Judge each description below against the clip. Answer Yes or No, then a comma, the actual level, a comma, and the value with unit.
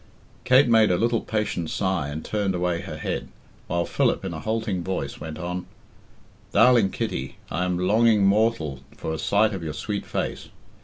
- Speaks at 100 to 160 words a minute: No, average, 175 wpm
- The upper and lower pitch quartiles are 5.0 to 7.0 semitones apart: No, average, 4.2 semitones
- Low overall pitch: Yes, very low, 95 Hz